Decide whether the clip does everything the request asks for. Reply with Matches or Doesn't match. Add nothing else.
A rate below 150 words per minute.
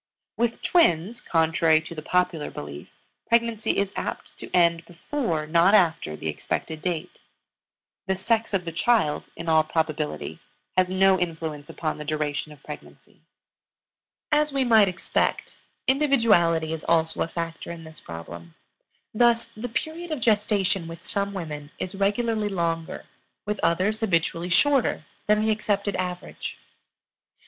Matches